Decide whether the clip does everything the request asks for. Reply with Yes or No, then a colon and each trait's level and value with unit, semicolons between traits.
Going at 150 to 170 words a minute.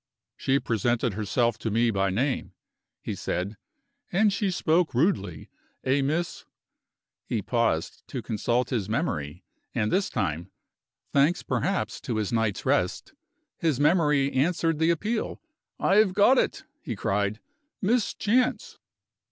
No: slow, 135 wpm